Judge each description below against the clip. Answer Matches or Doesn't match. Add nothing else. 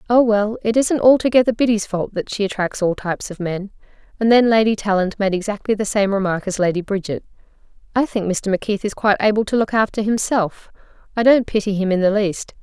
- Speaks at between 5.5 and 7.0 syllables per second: Matches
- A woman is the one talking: Matches